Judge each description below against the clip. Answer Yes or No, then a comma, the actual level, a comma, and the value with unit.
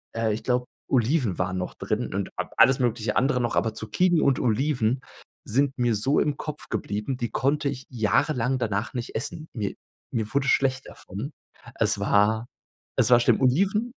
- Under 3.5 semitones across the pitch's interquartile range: No, average, 3.8 semitones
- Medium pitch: No, low, 125 Hz